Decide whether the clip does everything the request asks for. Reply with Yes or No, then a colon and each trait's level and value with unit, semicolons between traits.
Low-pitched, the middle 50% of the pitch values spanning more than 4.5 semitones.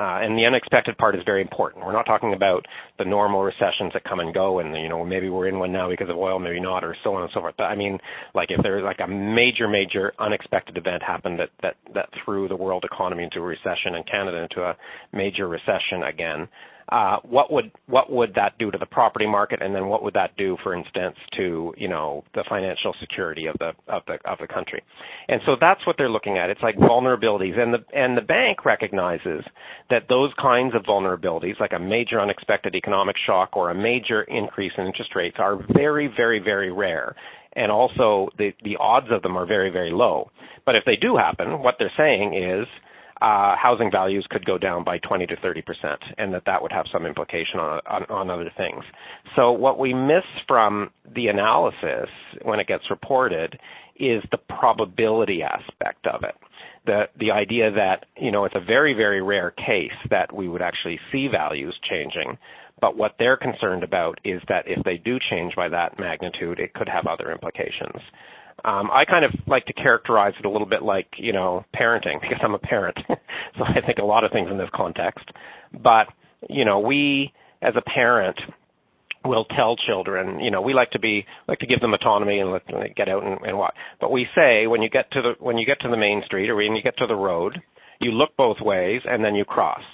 No: low, 105 Hz; average, 4.0 semitones